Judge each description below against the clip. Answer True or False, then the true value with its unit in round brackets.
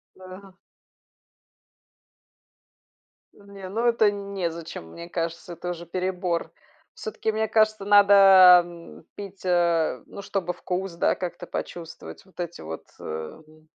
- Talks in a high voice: False (180 Hz)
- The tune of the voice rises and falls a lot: False (2.9 semitones)